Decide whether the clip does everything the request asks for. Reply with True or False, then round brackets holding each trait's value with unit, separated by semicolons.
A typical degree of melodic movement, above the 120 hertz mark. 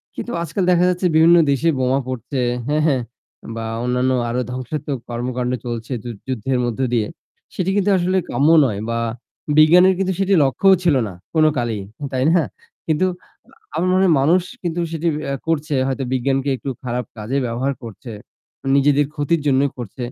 True (5.0 semitones; 140 Hz)